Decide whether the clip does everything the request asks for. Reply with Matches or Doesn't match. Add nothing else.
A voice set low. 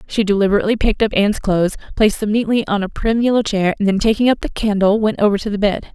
Doesn't match